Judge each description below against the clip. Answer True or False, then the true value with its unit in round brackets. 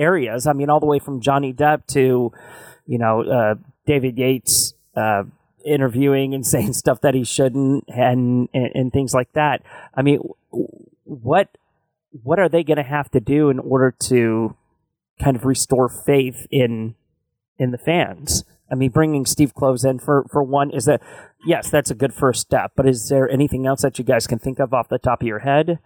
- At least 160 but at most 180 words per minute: False (195 wpm)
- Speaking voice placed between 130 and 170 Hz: True (135 Hz)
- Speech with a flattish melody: True (2.1 semitones)